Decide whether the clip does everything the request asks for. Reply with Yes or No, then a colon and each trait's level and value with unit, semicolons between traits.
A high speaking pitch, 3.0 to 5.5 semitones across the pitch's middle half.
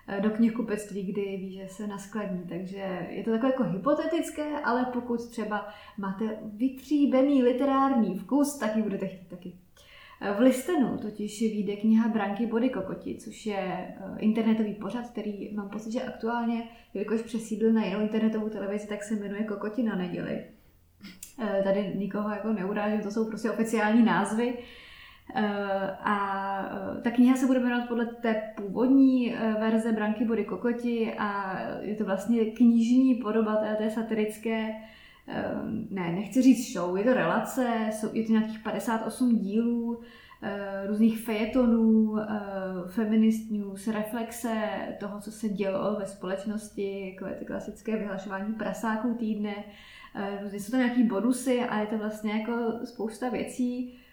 No: high, 220 Hz; narrow, 2.6 semitones